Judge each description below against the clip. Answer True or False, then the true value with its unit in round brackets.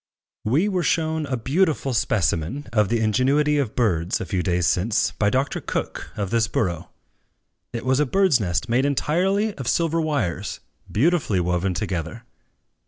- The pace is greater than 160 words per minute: False (155 wpm)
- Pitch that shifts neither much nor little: False (7.3 semitones)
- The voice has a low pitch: True (120 Hz)